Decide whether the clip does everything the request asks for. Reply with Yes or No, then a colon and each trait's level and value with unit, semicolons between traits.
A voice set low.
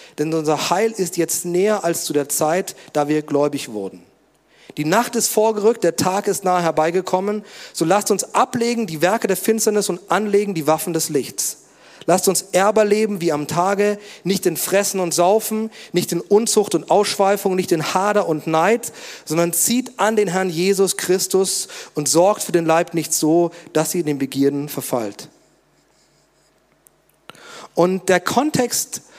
No: medium, 180 Hz